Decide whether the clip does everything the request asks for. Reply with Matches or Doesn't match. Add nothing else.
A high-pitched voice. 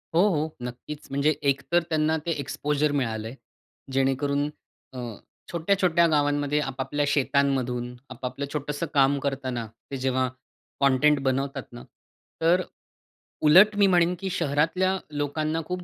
Doesn't match